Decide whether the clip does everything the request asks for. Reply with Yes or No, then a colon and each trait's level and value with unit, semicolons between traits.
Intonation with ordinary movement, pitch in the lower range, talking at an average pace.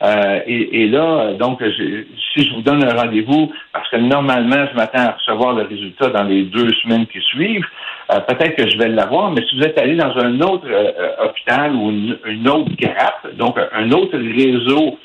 Yes: average, 4.4 semitones; low, 125 Hz; average, 205 wpm